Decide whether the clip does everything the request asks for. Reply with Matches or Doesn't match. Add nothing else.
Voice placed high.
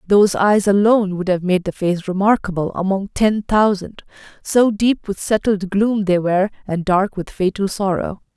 Matches